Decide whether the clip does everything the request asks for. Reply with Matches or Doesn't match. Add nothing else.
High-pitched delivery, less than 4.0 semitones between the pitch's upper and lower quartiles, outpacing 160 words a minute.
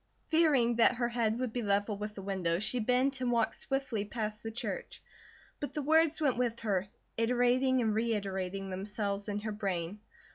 Matches